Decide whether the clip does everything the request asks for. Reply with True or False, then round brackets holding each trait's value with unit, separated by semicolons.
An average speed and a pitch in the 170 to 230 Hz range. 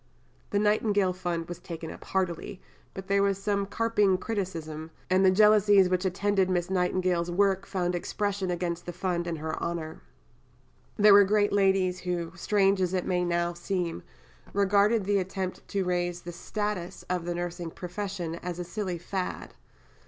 True (165 wpm; 185 Hz)